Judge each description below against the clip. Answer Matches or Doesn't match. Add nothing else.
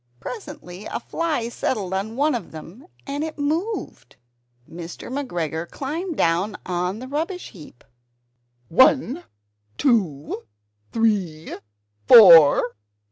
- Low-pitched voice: Doesn't match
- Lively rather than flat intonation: Matches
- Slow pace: Matches